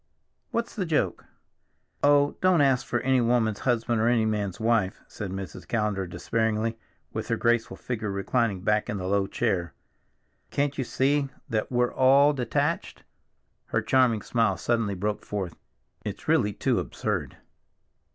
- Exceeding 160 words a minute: No, average, 150 wpm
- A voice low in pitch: Yes, low, 115 Hz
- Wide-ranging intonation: No, average, 3.9 semitones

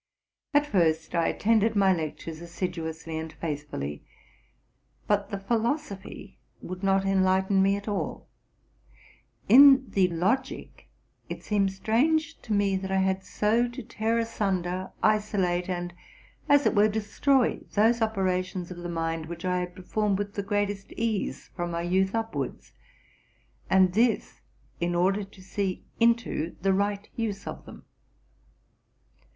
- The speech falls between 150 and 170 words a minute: No, average, 140 wpm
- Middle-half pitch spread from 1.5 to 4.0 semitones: Yes, average, 3.4 semitones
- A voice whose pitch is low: No, high, 195 Hz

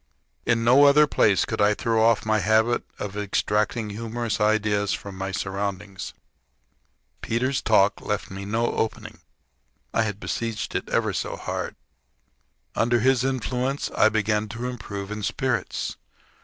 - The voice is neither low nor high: No, low, 110 Hz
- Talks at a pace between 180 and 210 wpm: No, average, 140 wpm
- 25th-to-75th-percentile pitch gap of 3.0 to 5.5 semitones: No, narrow, 2.4 semitones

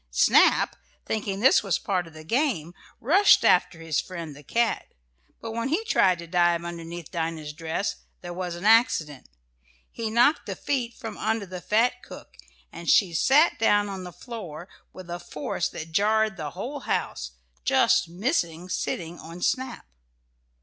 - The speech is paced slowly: No, average, 165 wpm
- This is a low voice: No, medium, 185 Hz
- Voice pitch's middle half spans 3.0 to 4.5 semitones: No, average, 5.2 semitones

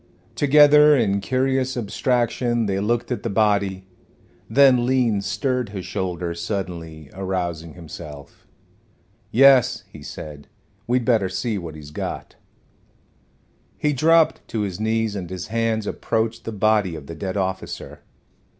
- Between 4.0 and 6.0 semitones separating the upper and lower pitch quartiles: Yes, average, 4.9 semitones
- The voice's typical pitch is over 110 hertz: No, low, 105 Hz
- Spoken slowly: Yes, slow, 130 wpm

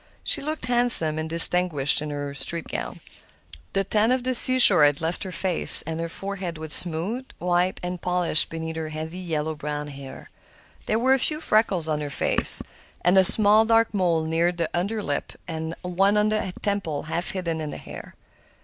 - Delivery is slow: No, average, 190 wpm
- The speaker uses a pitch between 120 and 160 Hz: No, medium, 175 Hz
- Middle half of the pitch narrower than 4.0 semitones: No, average, 4.3 semitones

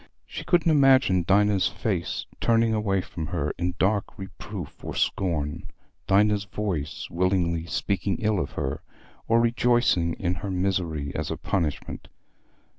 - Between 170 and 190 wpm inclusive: No, slow, 135 wpm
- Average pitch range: Yes, average, 3.9 semitones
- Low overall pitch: Yes, very low, 95 Hz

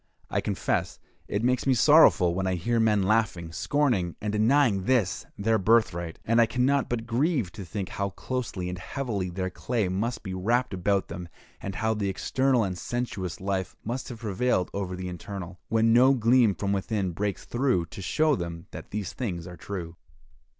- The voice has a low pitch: Yes, low, 105 Hz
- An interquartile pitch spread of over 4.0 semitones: Yes, average, 4.6 semitones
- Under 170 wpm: No, average, 185 wpm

